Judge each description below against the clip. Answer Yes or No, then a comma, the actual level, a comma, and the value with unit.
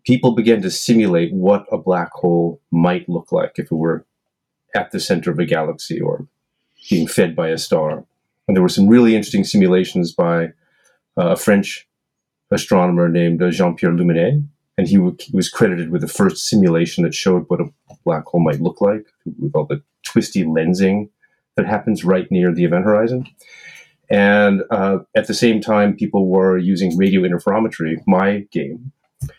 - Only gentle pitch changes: No, average, 4.6 semitones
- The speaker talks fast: No, average, 175 wpm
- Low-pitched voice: Yes, very low, 95 Hz